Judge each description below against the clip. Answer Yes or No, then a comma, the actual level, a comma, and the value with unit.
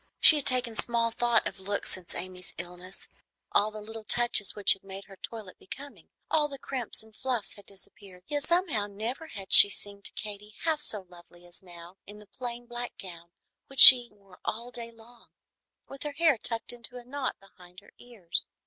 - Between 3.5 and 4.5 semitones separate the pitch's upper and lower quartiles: Yes, average, 4.0 semitones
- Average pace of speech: Yes, average, 195 wpm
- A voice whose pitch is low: No, high, 215 Hz